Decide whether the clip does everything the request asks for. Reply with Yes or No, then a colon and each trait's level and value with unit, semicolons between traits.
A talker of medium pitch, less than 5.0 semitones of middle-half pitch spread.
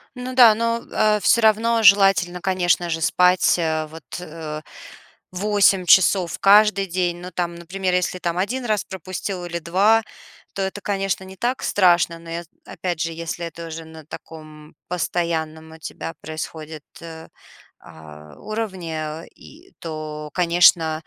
Yes: medium, 180 Hz; average, 3.3 semitones